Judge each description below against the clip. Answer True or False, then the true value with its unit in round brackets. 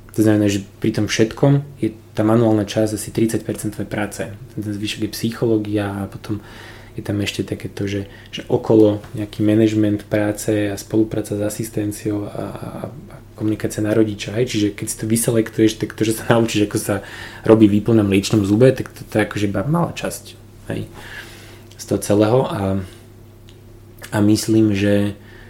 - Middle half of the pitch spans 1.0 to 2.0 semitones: True (1.4 semitones)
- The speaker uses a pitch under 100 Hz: False (110 Hz)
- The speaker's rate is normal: False (170 wpm)